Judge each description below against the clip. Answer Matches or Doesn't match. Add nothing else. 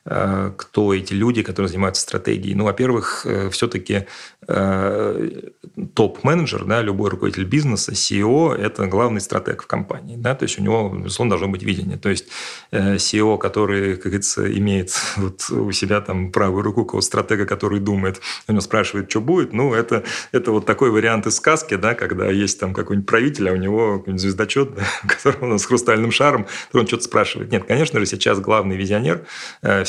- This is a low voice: Matches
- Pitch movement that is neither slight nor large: Doesn't match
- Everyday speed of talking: Doesn't match